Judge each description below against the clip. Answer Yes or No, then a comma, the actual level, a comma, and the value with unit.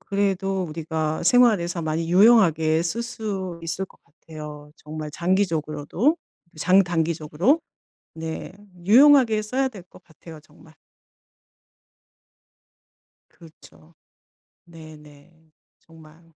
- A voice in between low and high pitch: Yes, medium, 170 Hz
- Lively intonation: No, average, 3.8 semitones